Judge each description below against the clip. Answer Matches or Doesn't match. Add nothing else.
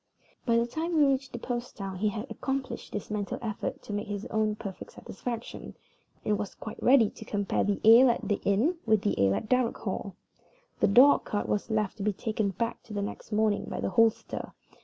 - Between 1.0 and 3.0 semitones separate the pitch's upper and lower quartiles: Matches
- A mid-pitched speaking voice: Doesn't match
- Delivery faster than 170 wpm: Matches